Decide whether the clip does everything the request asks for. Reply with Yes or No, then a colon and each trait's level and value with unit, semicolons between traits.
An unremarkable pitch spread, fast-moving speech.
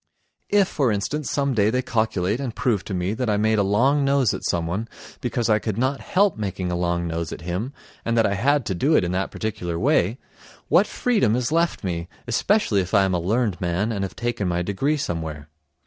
No: wide, 5.9 semitones; fast, 225 wpm